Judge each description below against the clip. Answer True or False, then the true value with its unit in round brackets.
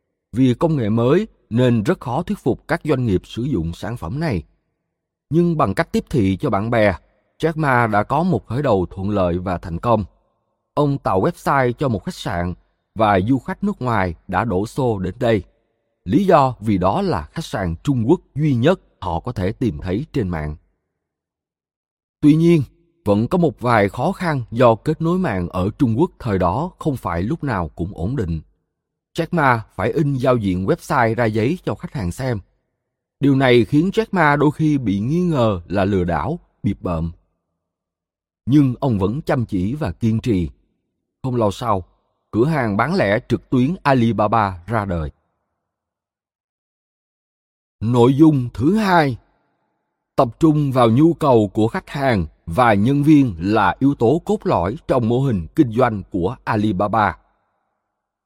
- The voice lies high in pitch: False (120 Hz)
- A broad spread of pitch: True (8.0 semitones)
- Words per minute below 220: True (175 wpm)